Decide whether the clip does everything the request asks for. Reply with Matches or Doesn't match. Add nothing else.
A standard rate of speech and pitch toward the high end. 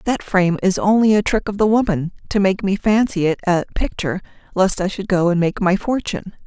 Doesn't match